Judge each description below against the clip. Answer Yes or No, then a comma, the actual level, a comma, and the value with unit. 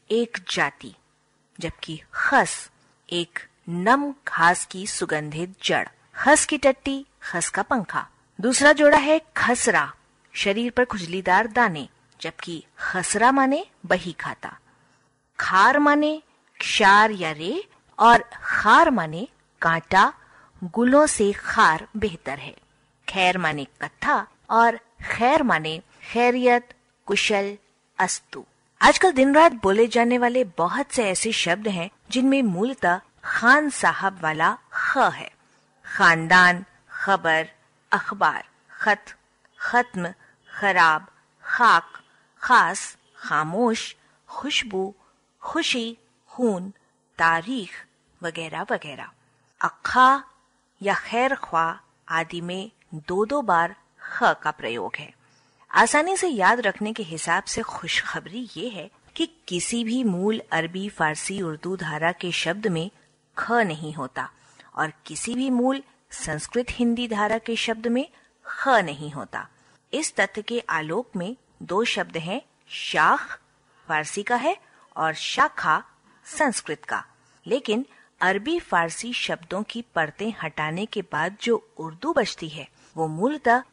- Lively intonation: Yes, wide, 6.6 semitones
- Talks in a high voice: Yes, high, 205 Hz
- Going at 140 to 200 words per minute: No, average, 120 wpm